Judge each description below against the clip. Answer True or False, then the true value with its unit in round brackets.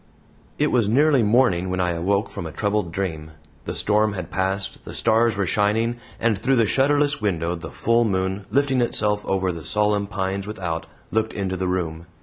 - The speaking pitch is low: True (100 Hz)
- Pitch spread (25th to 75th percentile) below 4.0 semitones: True (3.4 semitones)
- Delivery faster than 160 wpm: True (185 wpm)